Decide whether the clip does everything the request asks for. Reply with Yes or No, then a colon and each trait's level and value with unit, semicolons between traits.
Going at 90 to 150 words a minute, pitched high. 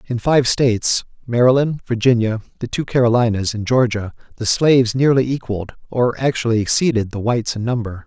No: average, 140 wpm; low, 120 Hz